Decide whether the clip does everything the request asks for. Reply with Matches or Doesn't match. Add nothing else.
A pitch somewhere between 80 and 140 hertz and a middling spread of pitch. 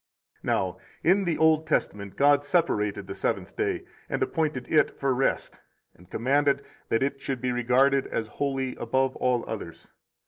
Matches